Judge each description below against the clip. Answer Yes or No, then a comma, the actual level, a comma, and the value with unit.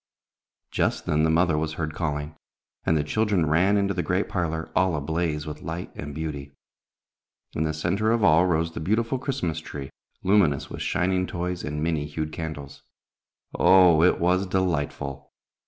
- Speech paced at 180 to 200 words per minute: No, average, 165 wpm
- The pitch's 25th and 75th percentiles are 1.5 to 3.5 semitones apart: Yes, average, 3.2 semitones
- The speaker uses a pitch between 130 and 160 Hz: No, very low, 80 Hz